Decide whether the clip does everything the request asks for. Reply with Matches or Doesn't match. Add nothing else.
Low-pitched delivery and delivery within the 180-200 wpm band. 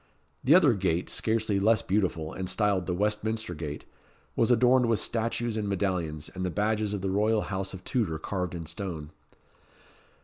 Doesn't match